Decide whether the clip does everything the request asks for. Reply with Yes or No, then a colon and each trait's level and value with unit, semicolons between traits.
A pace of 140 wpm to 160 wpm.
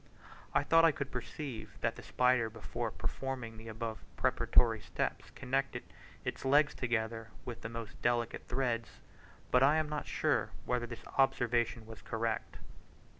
Yes: average, 150 wpm